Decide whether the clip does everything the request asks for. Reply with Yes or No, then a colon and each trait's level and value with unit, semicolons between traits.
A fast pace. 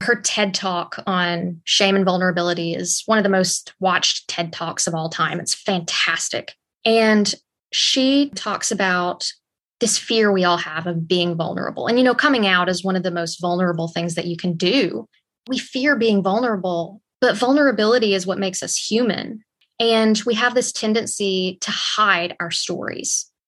No: average, 175 wpm